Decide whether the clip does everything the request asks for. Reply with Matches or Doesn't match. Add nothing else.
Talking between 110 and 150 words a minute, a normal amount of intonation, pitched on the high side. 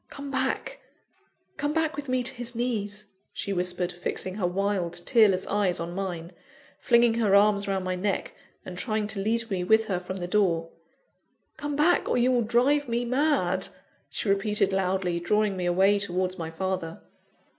Doesn't match